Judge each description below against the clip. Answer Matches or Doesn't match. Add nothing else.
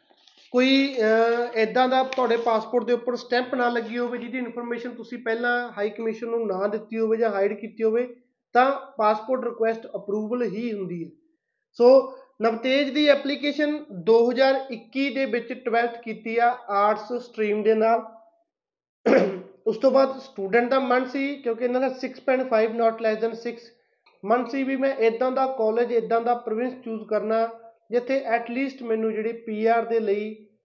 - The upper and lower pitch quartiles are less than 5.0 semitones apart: Matches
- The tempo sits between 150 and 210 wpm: Matches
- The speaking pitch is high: Matches